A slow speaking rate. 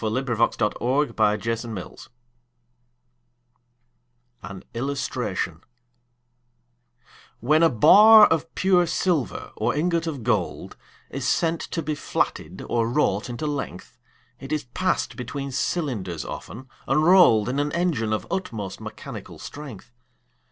Yes: slow, 120 wpm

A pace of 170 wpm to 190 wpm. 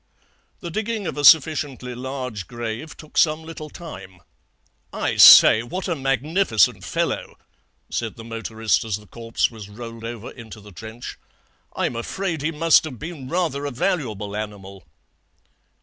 No: average, 150 wpm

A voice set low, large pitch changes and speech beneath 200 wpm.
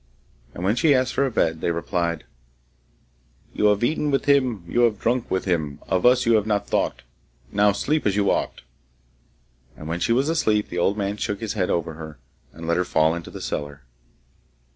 No: low, 100 Hz; wide, 6.0 semitones; fast, 205 wpm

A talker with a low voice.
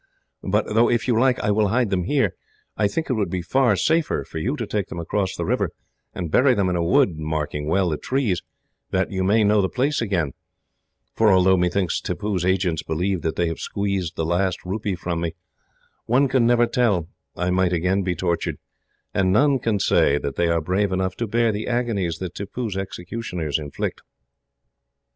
Yes: very low, 95 Hz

